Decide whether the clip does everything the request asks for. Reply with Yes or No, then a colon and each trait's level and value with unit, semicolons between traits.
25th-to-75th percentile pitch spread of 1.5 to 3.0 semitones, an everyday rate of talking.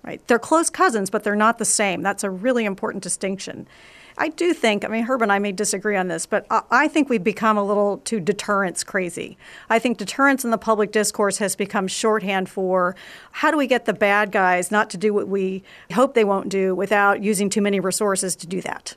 No: narrow, 2.4 semitones; fast, 225 wpm